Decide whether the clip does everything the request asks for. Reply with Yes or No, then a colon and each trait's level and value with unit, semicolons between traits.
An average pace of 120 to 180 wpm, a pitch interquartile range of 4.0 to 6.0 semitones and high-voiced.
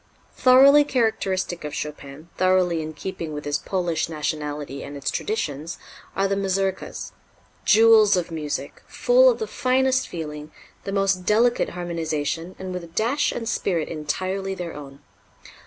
No: average, 145 wpm; wide, 5.5 semitones; medium, 180 Hz